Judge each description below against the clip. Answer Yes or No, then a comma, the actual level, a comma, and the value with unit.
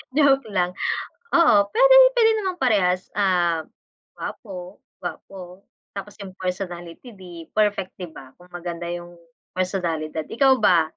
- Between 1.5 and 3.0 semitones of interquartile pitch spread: No, average, 3.6 semitones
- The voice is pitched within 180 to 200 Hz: Yes, medium, 185 Hz